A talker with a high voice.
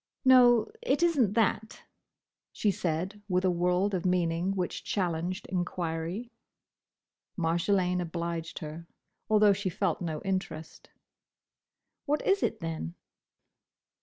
No: medium, 180 Hz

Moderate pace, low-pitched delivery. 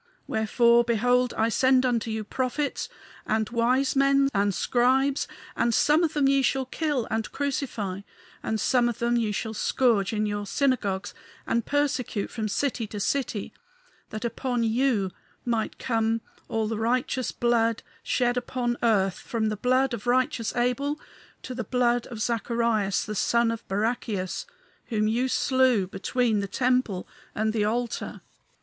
No: average, 155 wpm; high, 235 Hz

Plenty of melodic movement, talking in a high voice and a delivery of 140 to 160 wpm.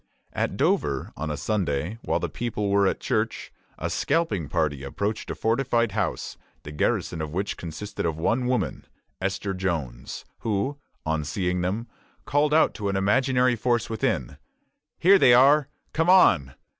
No: wide, 7.1 semitones; low, 100 Hz; average, 155 wpm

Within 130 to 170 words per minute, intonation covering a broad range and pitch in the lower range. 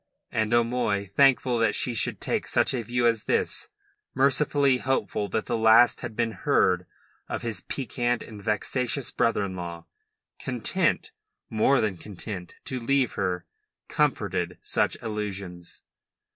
No: average, 140 wpm; average, 3.8 semitones; low, 110 Hz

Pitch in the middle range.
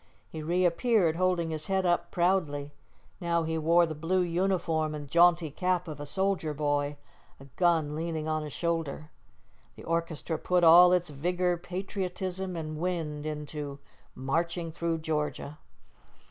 Yes: medium, 165 Hz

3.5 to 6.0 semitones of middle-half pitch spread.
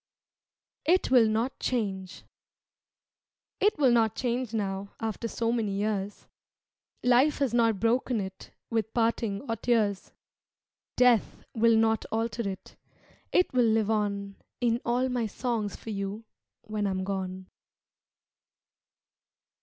No: average, 3.0 semitones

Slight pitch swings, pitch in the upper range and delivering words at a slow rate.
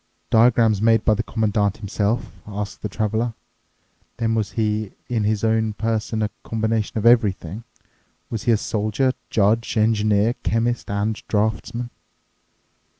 No: narrow, 1.4 semitones; low, 110 Hz; slow, 130 wpm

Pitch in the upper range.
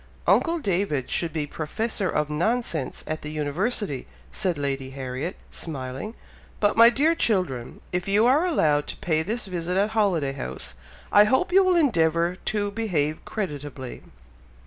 No: medium, 175 Hz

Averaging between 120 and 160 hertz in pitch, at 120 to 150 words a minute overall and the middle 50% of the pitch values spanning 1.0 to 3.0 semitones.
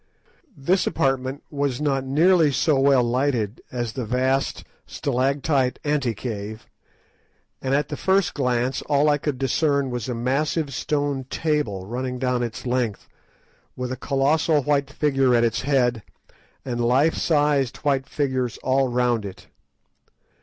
Yes: low, 135 Hz; average, 140 wpm; average, 2.7 semitones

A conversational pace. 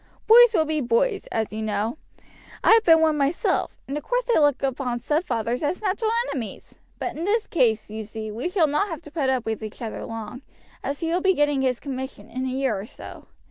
No: fast, 220 wpm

